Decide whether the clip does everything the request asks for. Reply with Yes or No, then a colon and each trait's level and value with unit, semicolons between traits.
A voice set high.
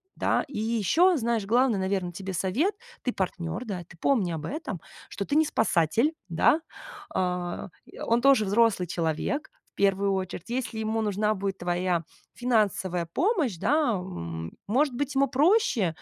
Yes: high, 210 Hz